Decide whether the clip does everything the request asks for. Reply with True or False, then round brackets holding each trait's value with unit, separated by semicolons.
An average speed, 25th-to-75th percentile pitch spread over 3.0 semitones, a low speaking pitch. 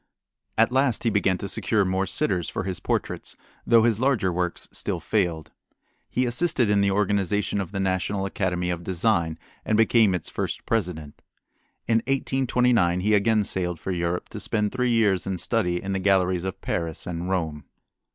True (175 wpm; 3.9 semitones; 95 Hz)